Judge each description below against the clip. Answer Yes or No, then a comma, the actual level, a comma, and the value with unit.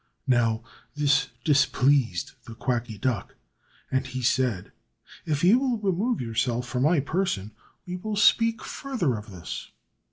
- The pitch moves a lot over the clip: Yes, wide, 7.4 semitones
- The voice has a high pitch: No, low, 130 Hz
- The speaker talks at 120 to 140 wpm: Yes, slow, 135 wpm